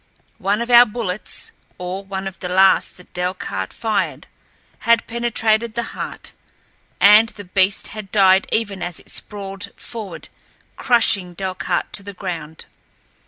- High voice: Yes, high, 195 Hz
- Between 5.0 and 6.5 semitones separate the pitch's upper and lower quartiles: No, average, 3.0 semitones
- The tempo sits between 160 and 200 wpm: No, average, 140 wpm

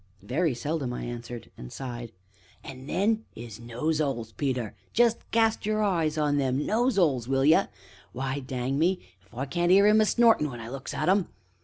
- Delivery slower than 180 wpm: No, average, 185 wpm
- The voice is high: No, medium, 140 Hz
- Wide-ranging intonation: Yes, wide, 7.1 semitones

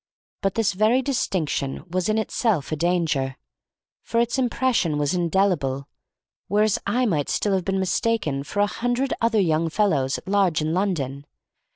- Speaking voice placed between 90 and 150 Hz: No, high, 190 Hz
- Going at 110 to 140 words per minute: No, average, 160 wpm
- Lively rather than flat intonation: Yes, wide, 5.8 semitones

